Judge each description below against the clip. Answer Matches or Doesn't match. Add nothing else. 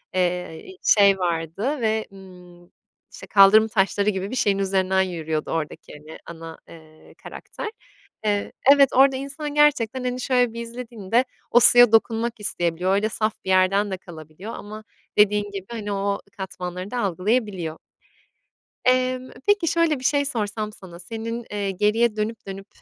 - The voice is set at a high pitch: Matches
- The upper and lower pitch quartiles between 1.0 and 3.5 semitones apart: Doesn't match